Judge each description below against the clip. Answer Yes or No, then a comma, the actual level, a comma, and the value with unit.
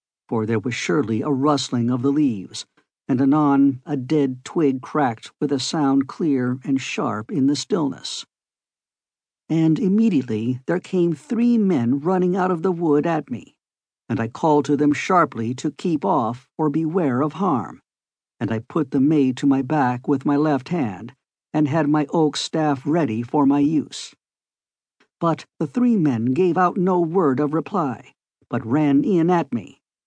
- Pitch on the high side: No, medium, 145 Hz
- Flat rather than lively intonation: No, average, 3.4 semitones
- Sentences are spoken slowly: No, average, 170 wpm